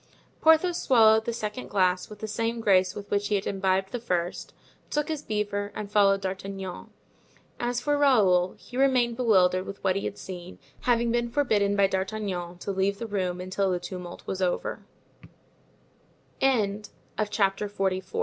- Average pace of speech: Yes, average, 160 wpm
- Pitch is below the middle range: No, high, 200 Hz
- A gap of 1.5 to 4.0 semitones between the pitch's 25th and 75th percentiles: Yes, average, 3.3 semitones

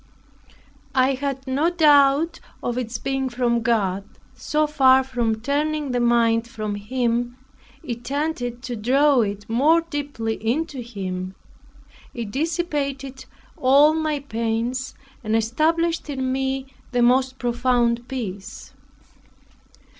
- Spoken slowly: Yes, slow, 115 wpm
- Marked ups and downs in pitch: No, average, 3.4 semitones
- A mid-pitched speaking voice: No, very high, 255 Hz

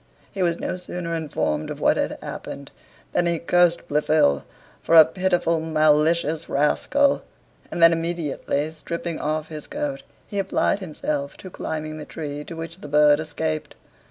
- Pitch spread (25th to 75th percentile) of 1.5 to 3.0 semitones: Yes, narrow, 2.4 semitones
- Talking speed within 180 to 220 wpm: No, average, 155 wpm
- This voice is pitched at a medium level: Yes, medium, 160 Hz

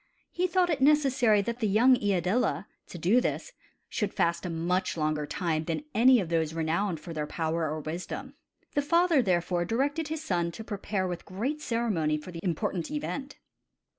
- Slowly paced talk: No, average, 180 wpm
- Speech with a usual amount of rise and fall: No, wide, 7.6 semitones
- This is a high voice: Yes, high, 195 Hz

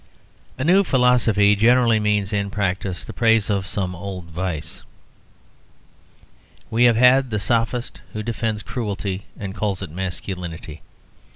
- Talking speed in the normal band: No, slow, 130 wpm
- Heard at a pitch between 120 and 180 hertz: No, low, 105 Hz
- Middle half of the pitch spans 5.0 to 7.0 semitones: No, average, 3.6 semitones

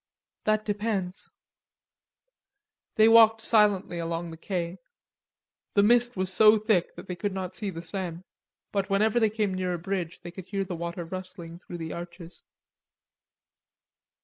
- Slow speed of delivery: No, average, 145 wpm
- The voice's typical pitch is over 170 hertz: Yes, medium, 185 Hz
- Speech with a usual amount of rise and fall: Yes, average, 3.5 semitones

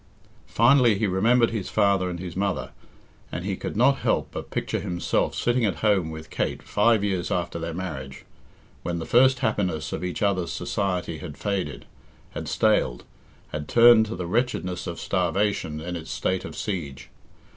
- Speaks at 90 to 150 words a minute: No, average, 170 wpm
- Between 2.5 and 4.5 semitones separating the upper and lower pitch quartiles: Yes, average, 4.0 semitones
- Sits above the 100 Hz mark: No, very low, 95 Hz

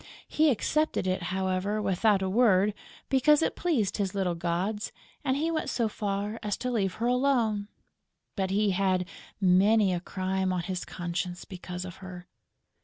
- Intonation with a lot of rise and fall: No, average, 3.3 semitones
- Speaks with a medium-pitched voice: No, high, 195 Hz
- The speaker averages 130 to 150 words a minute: No, average, 170 wpm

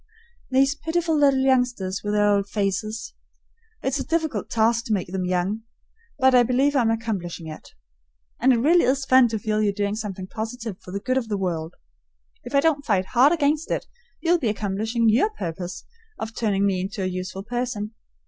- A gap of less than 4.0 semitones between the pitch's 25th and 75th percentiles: No, average, 5.0 semitones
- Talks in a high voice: Yes, high, 225 Hz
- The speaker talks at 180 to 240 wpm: Yes, average, 190 wpm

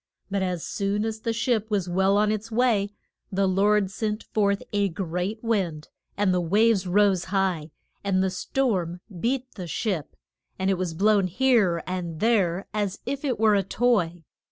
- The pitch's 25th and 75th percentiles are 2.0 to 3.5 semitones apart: Yes, average, 3.0 semitones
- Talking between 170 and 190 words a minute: Yes, average, 175 wpm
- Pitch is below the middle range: No, high, 200 Hz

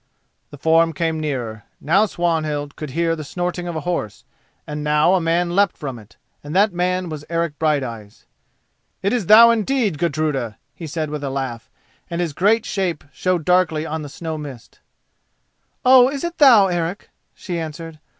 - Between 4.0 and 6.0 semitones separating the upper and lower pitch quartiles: No, average, 3.5 semitones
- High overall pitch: No, medium, 165 Hz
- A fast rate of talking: No, average, 175 wpm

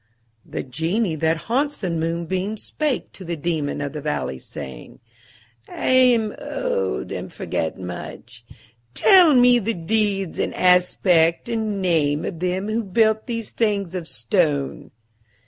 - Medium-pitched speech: Yes, medium, 180 Hz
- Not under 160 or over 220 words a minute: No, average, 140 wpm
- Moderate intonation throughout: No, wide, 5.7 semitones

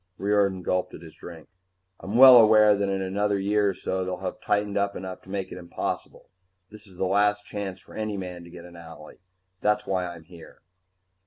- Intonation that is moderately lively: No, narrow, 2.3 semitones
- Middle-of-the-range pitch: No, very low, 95 Hz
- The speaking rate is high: Yes, fast, 210 wpm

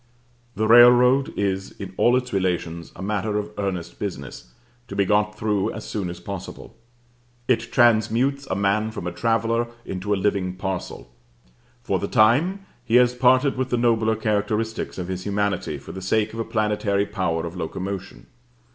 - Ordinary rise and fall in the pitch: Yes, average, 3.4 semitones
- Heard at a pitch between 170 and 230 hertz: No, low, 105 Hz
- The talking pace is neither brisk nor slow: Yes, average, 170 wpm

